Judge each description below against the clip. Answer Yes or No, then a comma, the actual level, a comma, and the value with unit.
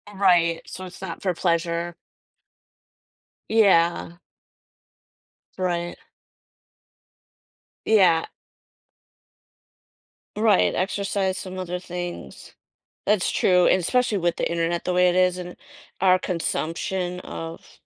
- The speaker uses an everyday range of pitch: No, narrow, 1.6 semitones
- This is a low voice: No, medium, 180 Hz